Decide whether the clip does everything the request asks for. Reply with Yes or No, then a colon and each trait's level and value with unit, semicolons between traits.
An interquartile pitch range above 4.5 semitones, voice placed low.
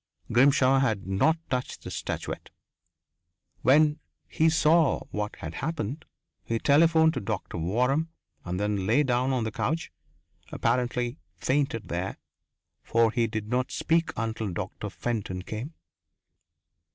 Yes: wide, 5.5 semitones; low, 120 Hz